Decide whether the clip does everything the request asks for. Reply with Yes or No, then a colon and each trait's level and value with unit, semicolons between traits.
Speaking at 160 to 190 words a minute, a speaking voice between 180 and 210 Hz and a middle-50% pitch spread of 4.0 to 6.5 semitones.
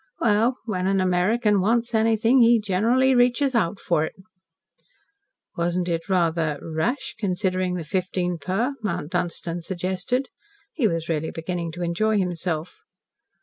No: slow, 135 wpm; medium, 185 Hz; average, 4.6 semitones